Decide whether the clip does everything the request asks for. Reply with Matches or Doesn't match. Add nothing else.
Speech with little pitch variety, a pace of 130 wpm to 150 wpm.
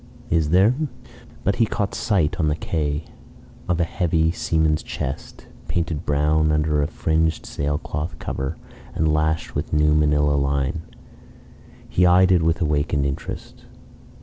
Matches